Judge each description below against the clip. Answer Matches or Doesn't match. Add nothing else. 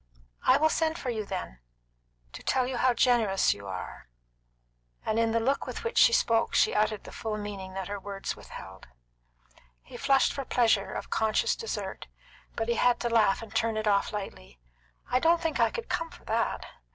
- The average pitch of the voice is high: Matches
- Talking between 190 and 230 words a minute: Matches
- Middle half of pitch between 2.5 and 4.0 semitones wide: Doesn't match